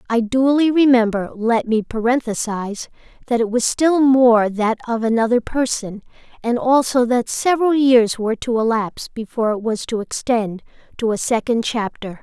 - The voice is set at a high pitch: Yes, high, 235 Hz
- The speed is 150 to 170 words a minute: Yes, average, 155 wpm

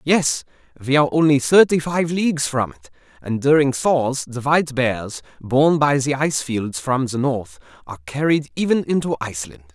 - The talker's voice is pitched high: No, low, 135 Hz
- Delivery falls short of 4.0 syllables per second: No, 5.3 syllables/s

